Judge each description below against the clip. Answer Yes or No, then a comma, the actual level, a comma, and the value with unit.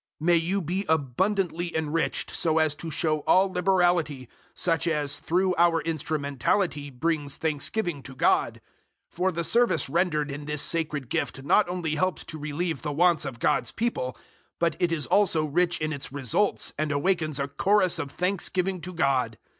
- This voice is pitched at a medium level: Yes, medium, 160 Hz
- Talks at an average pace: Yes, average, 170 wpm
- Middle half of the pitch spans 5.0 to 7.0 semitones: No, average, 3.6 semitones